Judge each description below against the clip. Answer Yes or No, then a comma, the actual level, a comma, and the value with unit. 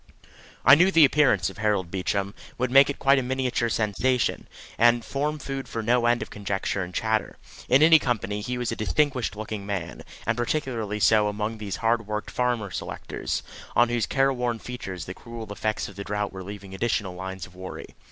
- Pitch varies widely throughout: No, average, 3.7 semitones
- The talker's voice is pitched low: Yes, low, 110 Hz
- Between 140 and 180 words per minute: No, average, 190 wpm